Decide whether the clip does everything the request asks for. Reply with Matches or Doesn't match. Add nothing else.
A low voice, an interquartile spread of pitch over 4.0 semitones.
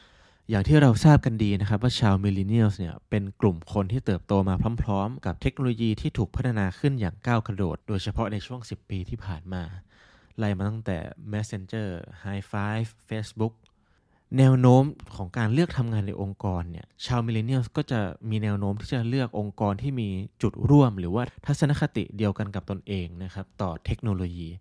Doesn't match